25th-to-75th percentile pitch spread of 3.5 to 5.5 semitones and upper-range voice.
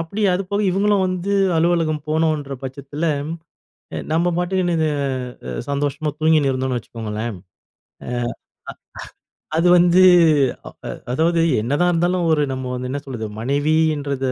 No: average, 4.2 semitones; medium, 155 Hz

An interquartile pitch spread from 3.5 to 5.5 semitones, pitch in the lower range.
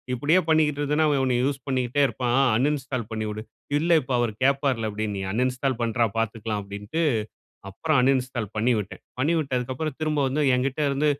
Yes: average, 4.2 semitones; low, 130 Hz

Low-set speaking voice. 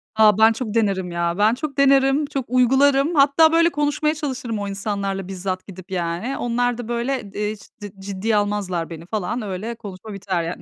No: high, 220 Hz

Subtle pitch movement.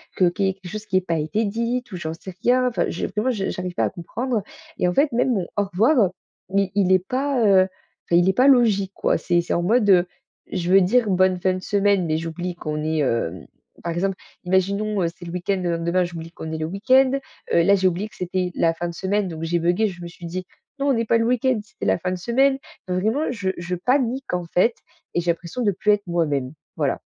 No: average, 4.0 semitones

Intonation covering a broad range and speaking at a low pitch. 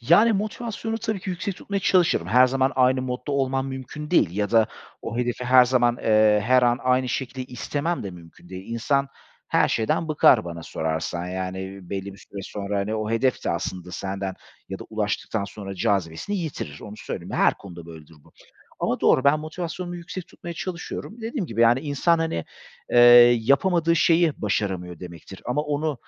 Yes: wide, 8.0 semitones; low, 125 Hz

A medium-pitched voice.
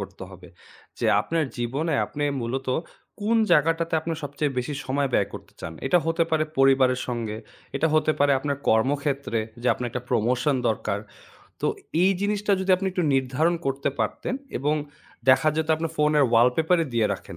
Yes: medium, 145 Hz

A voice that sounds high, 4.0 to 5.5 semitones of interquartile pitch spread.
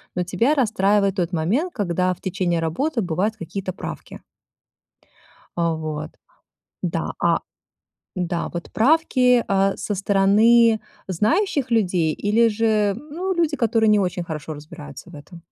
Yes: high, 195 Hz; average, 5.0 semitones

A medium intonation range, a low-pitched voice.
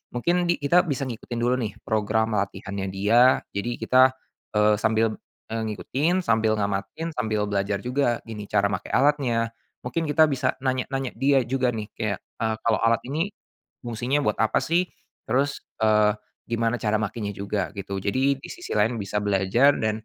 Yes: average, 4.0 semitones; low, 115 Hz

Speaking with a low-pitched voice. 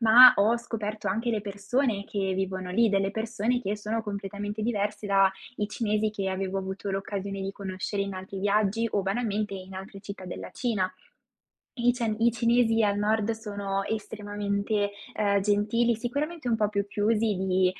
No: high, 205 Hz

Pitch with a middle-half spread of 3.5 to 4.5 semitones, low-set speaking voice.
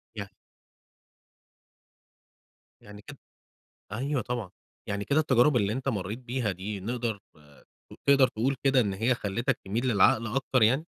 Yes: average, 4.1 semitones; low, 115 Hz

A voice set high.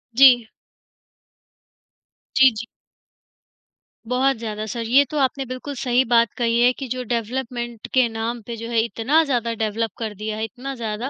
Yes: high, 235 Hz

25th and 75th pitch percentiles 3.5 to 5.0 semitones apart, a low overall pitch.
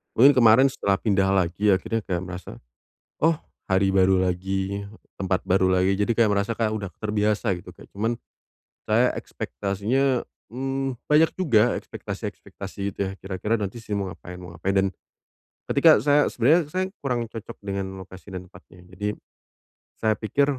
Yes: average, 3.8 semitones; low, 100 Hz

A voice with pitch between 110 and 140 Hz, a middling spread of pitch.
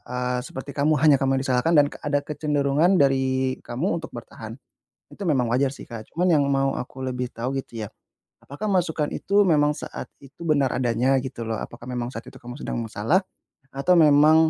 Yes: low, 135 Hz; average, 3.4 semitones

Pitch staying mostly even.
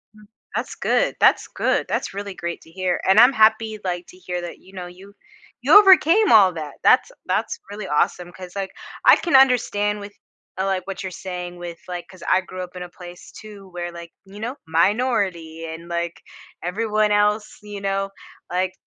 No: average, 3.0 semitones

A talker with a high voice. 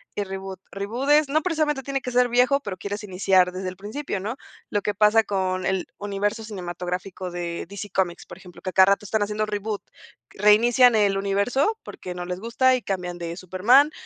Yes: high, 205 Hz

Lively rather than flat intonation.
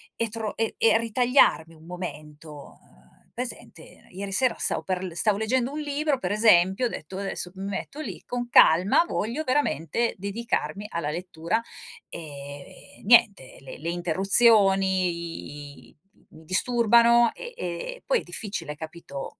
Yes: wide, 5.7 semitones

